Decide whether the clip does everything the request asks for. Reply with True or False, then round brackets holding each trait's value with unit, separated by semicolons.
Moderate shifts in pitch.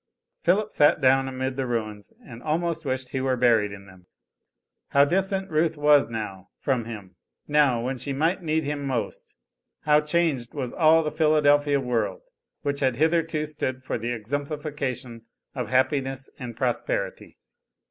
True (3.9 semitones)